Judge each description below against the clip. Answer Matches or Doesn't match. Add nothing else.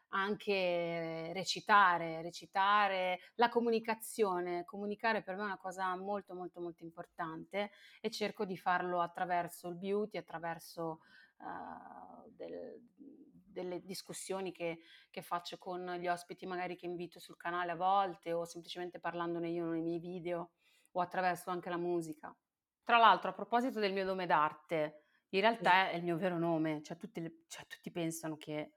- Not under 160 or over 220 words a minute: Doesn't match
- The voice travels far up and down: Doesn't match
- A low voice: Doesn't match